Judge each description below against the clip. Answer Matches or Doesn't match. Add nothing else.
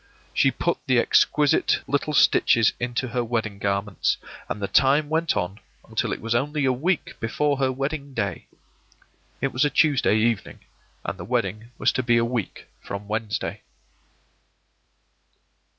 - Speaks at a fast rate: Doesn't match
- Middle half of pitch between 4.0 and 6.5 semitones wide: Matches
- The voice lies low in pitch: Matches